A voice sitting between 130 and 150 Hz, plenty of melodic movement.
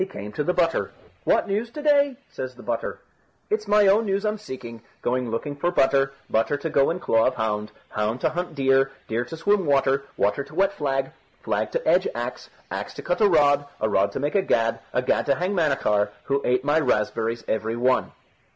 Yes: medium, 140 Hz; wide, 7.4 semitones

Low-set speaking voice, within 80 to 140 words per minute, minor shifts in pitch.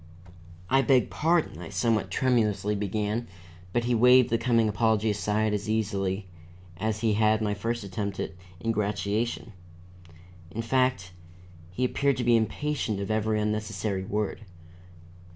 Yes: low, 110 Hz; slow, 135 wpm; narrow, 2.3 semitones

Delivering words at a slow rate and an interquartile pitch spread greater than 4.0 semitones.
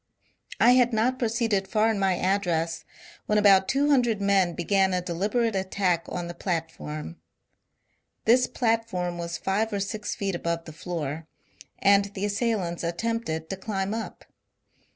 No: average, 150 wpm; average, 4.4 semitones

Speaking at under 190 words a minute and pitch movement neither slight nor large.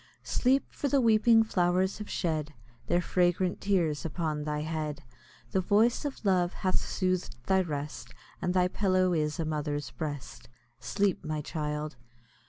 Yes: average, 150 wpm; average, 4.1 semitones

